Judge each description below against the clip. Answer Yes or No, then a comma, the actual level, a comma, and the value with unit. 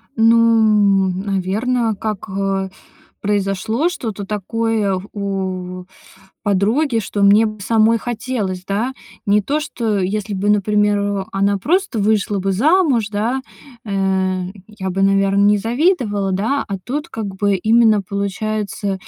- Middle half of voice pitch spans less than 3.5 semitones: Yes, narrow, 2.5 semitones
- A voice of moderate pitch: No, high, 205 Hz